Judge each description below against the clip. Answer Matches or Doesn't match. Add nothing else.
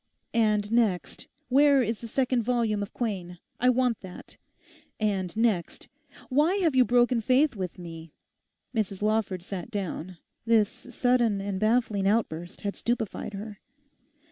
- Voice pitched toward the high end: Matches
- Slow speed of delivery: Matches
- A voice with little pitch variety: Doesn't match